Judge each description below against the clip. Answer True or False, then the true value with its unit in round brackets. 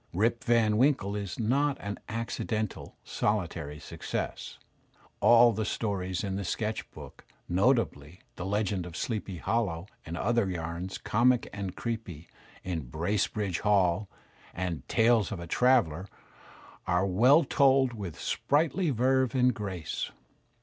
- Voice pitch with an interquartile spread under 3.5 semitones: False (4.7 semitones)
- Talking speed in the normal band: False (130 wpm)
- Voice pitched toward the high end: False (105 Hz)